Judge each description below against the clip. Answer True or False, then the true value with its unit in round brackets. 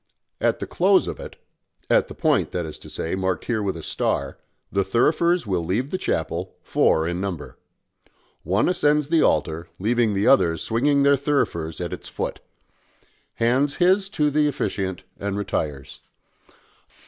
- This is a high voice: False (100 Hz)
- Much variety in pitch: True (8.5 semitones)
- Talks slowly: False (160 wpm)